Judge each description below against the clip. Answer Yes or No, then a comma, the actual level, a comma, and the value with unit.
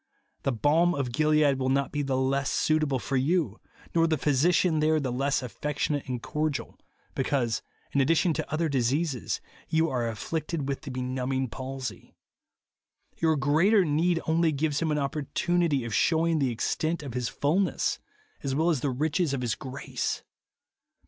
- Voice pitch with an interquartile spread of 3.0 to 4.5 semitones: Yes, average, 3.3 semitones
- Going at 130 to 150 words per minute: No, average, 165 wpm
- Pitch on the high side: No, medium, 145 Hz